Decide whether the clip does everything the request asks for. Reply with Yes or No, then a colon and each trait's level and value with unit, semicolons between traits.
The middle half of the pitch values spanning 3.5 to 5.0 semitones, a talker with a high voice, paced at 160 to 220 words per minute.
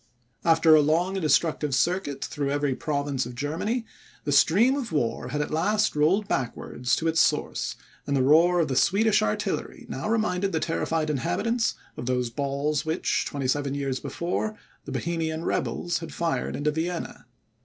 No: average, 3.8 semitones; medium, 155 Hz; average, 170 wpm